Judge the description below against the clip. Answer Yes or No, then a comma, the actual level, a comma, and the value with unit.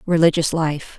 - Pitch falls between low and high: Yes, medium, 160 Hz